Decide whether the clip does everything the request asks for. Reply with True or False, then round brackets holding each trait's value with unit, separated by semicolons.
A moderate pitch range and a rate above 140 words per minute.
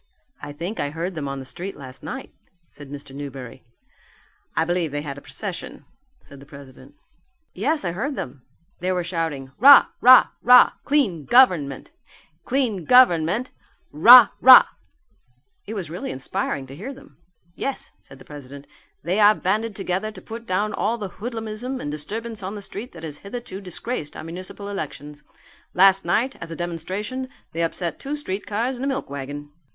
False (7.5 semitones; 170 wpm)